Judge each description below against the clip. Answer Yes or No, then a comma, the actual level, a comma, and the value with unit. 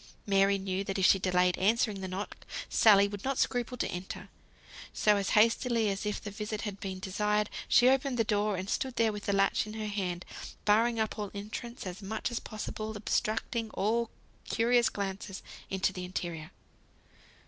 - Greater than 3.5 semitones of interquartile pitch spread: No, narrow, 2.5 semitones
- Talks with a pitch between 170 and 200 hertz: No, high, 210 Hz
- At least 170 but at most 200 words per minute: Yes, average, 185 wpm